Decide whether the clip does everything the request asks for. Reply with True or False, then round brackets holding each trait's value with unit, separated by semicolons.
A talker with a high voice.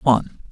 False (120 Hz)